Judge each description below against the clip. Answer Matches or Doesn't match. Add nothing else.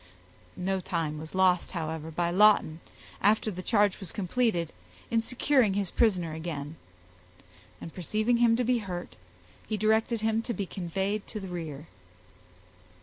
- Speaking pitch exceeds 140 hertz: Matches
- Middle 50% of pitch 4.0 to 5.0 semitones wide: Matches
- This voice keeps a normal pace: Matches